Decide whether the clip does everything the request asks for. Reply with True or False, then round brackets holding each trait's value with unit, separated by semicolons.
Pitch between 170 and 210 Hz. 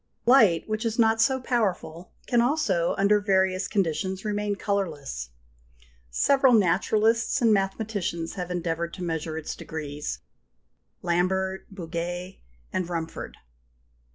True (190 Hz)